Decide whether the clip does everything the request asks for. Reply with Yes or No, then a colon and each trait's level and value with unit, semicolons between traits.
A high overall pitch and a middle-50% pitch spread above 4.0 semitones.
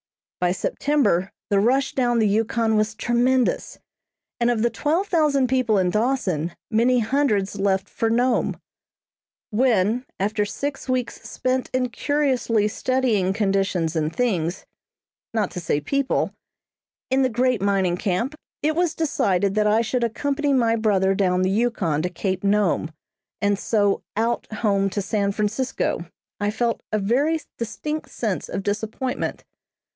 Yes: high, 220 Hz; average, 4.4 semitones